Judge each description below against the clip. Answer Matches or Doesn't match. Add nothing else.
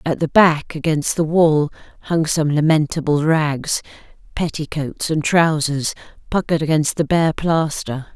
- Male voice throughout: Doesn't match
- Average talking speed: Doesn't match